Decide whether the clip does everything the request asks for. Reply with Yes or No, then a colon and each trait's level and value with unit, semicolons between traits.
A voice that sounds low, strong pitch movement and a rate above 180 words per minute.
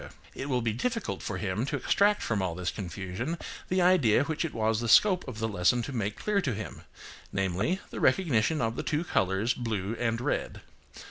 Yes: low, 115 Hz; wide, 7.0 semitones; average, 200 wpm